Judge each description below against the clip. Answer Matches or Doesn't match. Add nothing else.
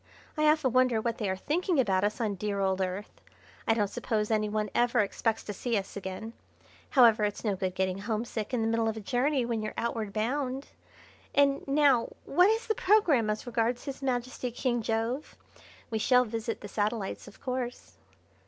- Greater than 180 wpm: Matches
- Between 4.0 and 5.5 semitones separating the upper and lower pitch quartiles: Doesn't match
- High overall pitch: Matches